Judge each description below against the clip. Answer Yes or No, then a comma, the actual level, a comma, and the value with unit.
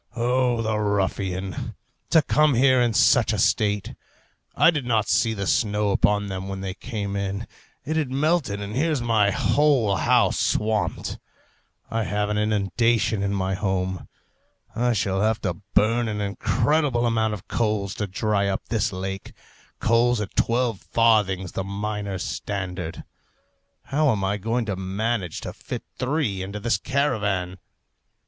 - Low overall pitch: Yes, low, 105 Hz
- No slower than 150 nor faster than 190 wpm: Yes, average, 155 wpm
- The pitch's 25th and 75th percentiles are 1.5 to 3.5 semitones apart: Yes, average, 3.2 semitones